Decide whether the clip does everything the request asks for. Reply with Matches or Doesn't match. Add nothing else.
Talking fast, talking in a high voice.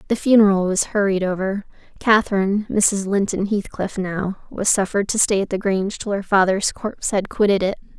Doesn't match